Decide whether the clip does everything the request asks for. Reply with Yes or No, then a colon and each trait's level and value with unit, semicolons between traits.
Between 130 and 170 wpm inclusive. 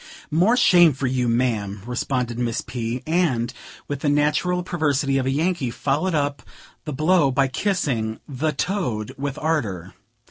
Yes: average, 150 wpm